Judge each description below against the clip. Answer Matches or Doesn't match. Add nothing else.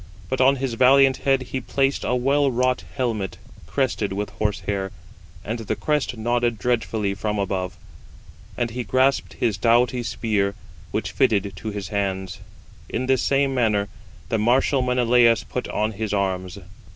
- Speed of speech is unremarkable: Matches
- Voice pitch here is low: Matches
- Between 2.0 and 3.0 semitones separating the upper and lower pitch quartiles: Doesn't match